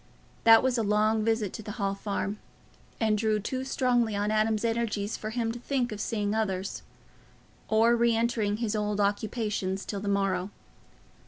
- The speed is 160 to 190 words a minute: Yes, average, 175 wpm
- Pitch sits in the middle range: No, high, 215 Hz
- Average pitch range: No, narrow, 1.9 semitones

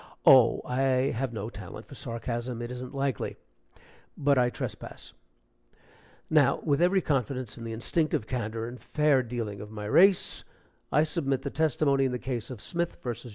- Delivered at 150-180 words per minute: Yes, average, 165 wpm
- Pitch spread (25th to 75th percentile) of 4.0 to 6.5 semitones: No, average, 3.2 semitones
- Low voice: Yes, low, 125 Hz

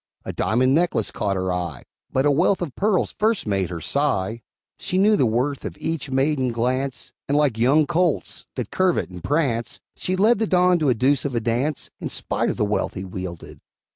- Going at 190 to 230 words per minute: Yes, average, 200 wpm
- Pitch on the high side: No, low, 135 Hz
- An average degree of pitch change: No, wide, 6.8 semitones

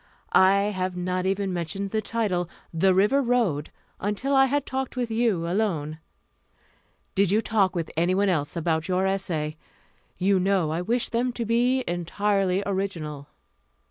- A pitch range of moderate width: Yes, average, 4.1 semitones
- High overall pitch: Yes, high, 195 Hz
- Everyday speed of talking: Yes, average, 150 wpm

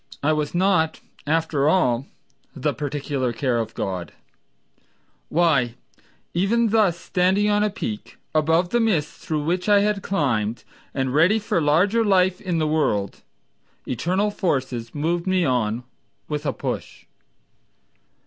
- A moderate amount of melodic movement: No, wide, 5.8 semitones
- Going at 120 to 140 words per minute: Yes, slow, 135 wpm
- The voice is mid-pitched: Yes, medium, 160 Hz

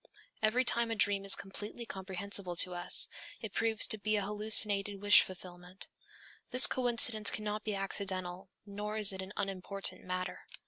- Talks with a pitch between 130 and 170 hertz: No, high, 200 Hz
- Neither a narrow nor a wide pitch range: No, narrow, 2.2 semitones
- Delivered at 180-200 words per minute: No, average, 155 wpm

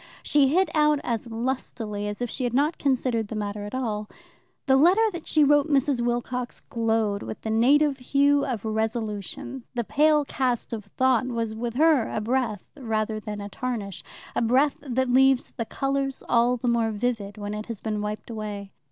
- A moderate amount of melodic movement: Yes, average, 3.8 semitones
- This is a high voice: Yes, high, 240 Hz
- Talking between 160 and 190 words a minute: Yes, average, 185 wpm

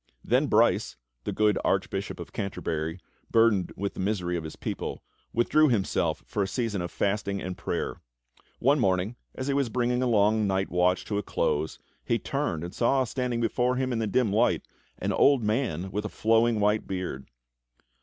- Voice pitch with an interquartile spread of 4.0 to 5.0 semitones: Yes, average, 4.3 semitones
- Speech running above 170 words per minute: Yes, average, 185 wpm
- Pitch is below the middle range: Yes, low, 105 Hz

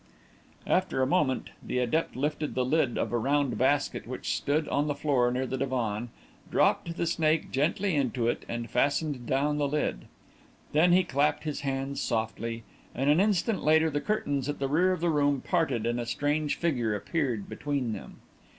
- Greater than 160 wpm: Yes, average, 185 wpm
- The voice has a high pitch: No, medium, 145 Hz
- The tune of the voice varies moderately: Yes, average, 3.8 semitones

